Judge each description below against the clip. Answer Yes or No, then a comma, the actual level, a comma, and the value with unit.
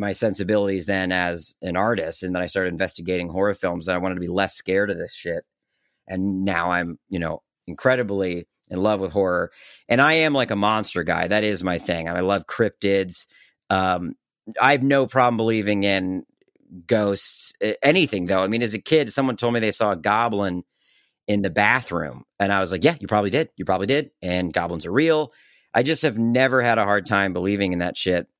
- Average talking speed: No, fast, 210 wpm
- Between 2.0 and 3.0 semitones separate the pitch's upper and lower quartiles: No, average, 3.5 semitones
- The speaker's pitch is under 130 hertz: Yes, low, 100 Hz